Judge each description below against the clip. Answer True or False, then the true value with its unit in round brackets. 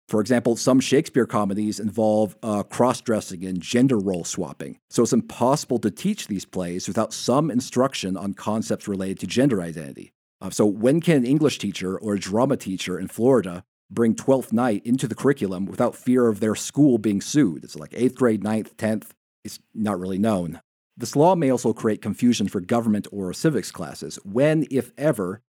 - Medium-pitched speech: False (110 Hz)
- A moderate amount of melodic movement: True (4.4 semitones)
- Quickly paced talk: False (185 wpm)